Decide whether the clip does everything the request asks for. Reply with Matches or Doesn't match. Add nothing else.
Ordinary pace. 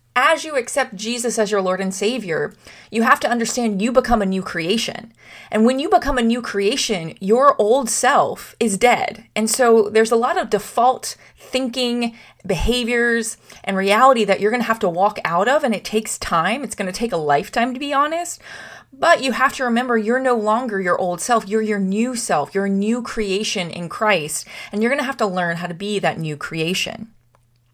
Doesn't match